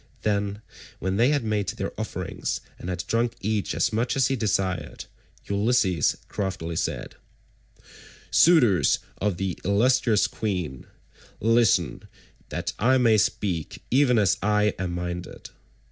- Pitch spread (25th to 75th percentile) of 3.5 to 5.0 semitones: Yes, average, 3.8 semitones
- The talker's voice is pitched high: No, low, 105 Hz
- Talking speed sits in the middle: No, slow, 130 wpm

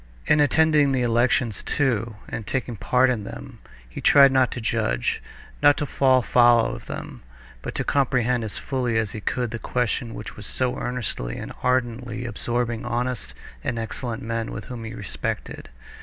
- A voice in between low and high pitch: No, low, 120 Hz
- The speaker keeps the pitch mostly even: Yes, narrow, 2.3 semitones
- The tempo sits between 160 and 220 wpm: Yes, average, 170 wpm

